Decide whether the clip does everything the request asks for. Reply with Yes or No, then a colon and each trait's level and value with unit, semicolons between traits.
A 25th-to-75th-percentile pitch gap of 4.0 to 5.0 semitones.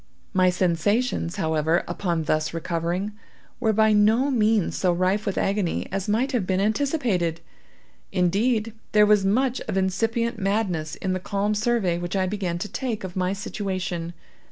No: average, 3.6 semitones